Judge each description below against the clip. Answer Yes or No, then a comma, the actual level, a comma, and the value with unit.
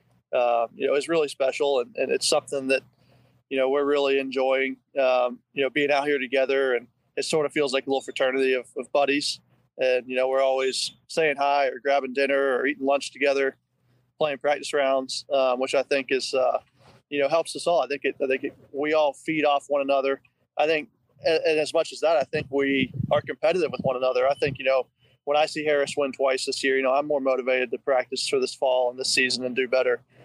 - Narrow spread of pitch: Yes, narrow, 1.7 semitones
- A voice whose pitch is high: No, low, 135 Hz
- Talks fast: Yes, fast, 235 wpm